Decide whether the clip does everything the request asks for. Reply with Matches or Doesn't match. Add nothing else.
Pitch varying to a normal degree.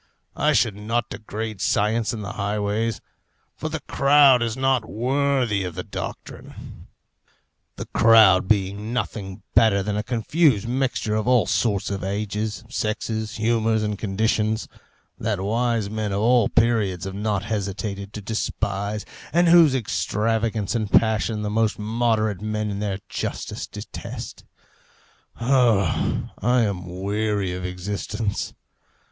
Doesn't match